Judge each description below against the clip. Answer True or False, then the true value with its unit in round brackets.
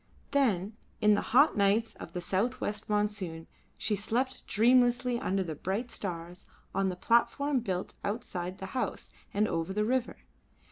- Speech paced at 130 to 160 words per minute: True (155 wpm)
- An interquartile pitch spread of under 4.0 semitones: False (4.3 semitones)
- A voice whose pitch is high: True (210 Hz)